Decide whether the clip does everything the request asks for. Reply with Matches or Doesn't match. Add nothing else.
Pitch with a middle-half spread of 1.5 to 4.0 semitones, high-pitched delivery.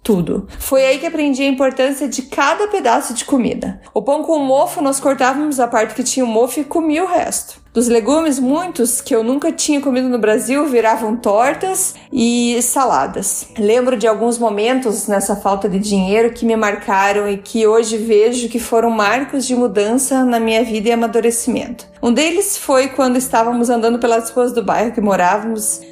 Matches